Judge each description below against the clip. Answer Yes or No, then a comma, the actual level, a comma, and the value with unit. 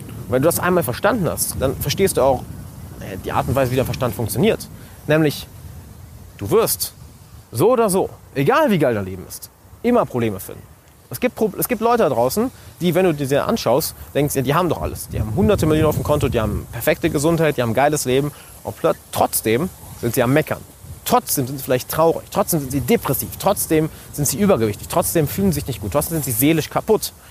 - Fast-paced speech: Yes, fast, 215 wpm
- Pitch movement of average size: No, wide, 6.3 semitones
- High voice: No, medium, 140 Hz